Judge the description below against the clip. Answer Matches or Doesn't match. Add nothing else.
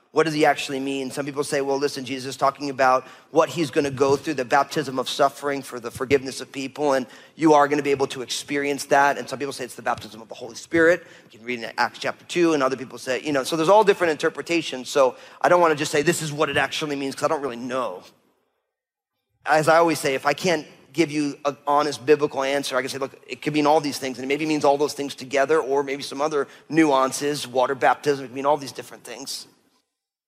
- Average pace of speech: Doesn't match